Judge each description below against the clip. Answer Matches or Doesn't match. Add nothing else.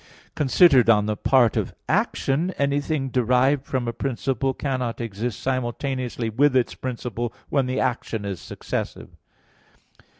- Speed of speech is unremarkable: Doesn't match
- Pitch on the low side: Matches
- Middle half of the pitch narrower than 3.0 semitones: Matches